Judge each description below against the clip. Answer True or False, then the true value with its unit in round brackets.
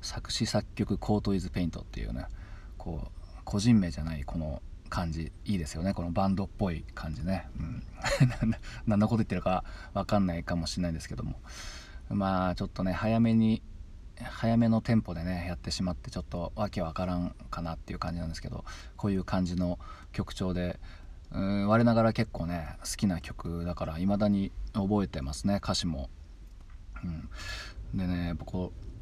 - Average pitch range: True (3.2 semitones)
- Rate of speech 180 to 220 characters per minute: False (335 characters per minute)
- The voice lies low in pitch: True (90 Hz)